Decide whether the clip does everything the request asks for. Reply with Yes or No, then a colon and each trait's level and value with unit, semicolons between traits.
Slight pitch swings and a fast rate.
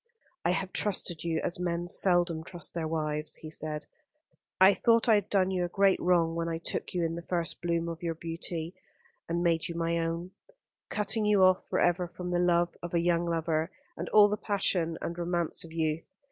Yes: narrow, 1.7 semitones; fast, 215 wpm